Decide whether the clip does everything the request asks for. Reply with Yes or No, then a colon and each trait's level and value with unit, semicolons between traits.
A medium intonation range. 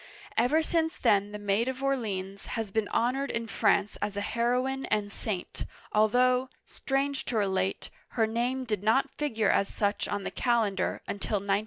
Yes: average, 3.9 semitones